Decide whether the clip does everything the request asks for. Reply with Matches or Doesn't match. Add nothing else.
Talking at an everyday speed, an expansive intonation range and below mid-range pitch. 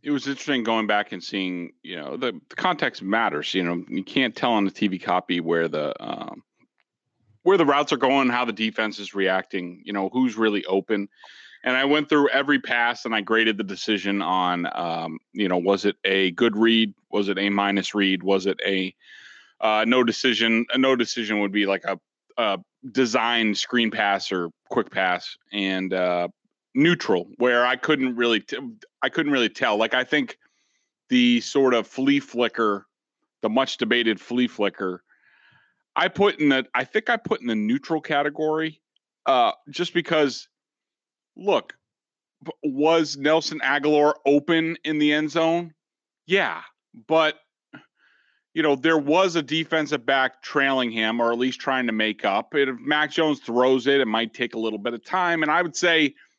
Matches